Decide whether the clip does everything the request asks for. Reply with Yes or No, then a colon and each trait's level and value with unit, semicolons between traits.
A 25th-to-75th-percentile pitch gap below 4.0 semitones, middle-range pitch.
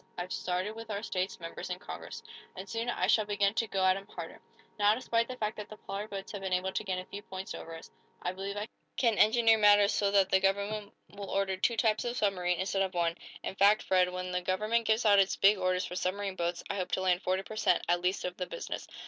No: narrow, 2.4 semitones; high, 195 Hz